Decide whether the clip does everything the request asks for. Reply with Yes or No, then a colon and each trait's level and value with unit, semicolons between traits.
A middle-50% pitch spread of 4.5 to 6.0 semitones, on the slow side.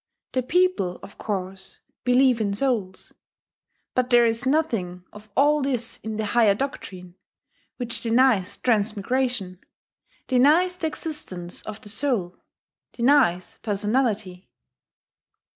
Yes: average, 5.0 semitones; slow, 110 wpm